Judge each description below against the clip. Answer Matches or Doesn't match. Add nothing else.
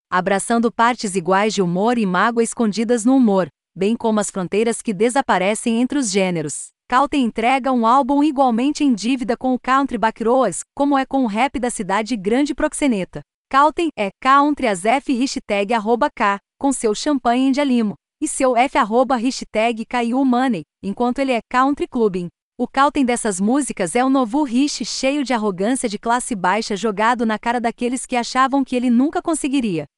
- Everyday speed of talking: Matches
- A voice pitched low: Doesn't match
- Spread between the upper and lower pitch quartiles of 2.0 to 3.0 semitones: Doesn't match